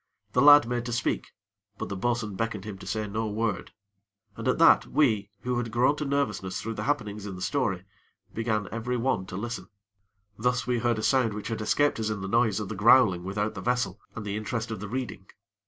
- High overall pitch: No, low, 110 Hz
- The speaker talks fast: Yes, fast, 225 wpm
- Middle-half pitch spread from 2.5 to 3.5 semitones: Yes, average, 3.2 semitones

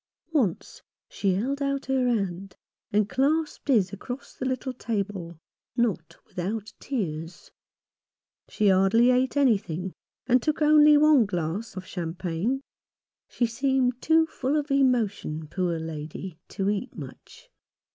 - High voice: Yes, high, 225 Hz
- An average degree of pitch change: No, wide, 6.2 semitones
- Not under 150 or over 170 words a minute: No, slow, 135 wpm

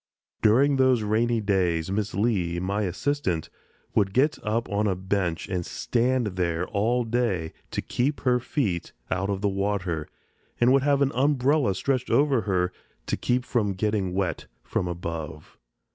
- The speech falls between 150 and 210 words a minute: Yes, average, 160 wpm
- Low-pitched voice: Yes, low, 105 Hz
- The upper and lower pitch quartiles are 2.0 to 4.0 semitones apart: No, average, 5.2 semitones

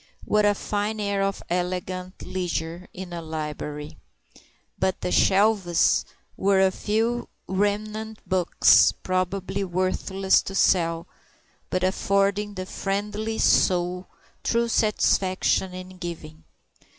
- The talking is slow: Yes, slow, 110 wpm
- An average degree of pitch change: No, narrow, 2.2 semitones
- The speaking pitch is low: No, high, 190 Hz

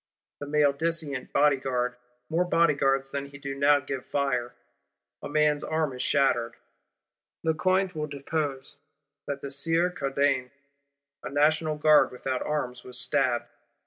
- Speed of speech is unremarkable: No, slow, 130 wpm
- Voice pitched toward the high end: No, medium, 140 Hz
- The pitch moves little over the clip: Yes, narrow, 2.2 semitones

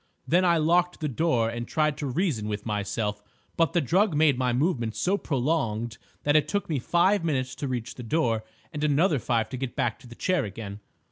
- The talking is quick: Yes, fast, 210 wpm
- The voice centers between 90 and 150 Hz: Yes, low, 135 Hz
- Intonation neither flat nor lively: No, wide, 6.0 semitones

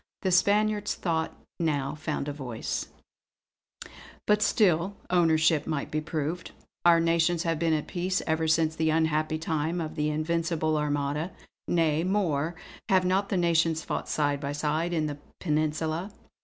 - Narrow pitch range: Yes, narrow, 2.2 semitones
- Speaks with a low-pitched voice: No, medium, 160 Hz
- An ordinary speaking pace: Yes, average, 150 wpm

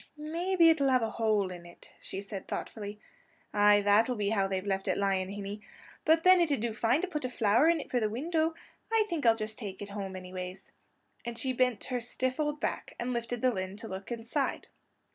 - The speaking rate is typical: No, fast, 220 wpm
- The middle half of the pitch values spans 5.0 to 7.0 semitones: Yes, average, 5.3 semitones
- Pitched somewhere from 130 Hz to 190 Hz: No, high, 225 Hz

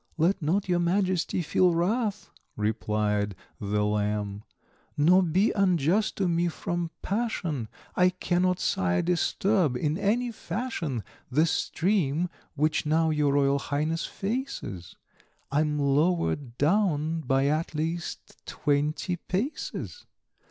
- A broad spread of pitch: No, average, 4.5 semitones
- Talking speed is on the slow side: Yes, slow, 115 wpm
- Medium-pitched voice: Yes, medium, 165 Hz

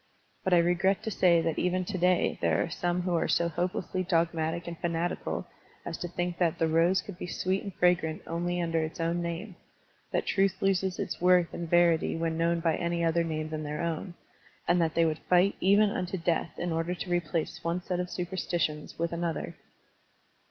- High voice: No, medium, 170 Hz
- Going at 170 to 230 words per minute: Yes, average, 200 wpm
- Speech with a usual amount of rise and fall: No, narrow, 1.5 semitones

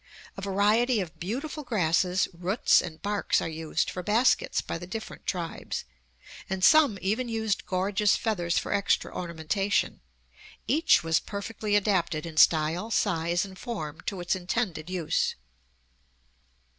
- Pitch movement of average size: Yes, average, 4.1 semitones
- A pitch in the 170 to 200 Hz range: Yes, high, 190 Hz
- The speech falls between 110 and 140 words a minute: Yes, slow, 135 wpm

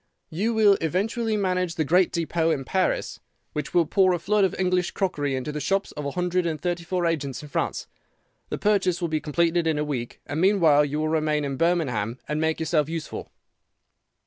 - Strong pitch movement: No, average, 3.4 semitones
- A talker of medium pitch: Yes, medium, 165 Hz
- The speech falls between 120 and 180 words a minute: No, average, 200 wpm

